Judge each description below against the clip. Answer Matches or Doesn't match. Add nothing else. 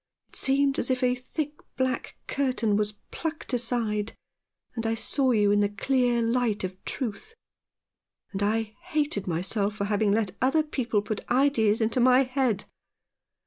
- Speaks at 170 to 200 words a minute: Doesn't match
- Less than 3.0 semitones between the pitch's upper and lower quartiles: Doesn't match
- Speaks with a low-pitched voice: Doesn't match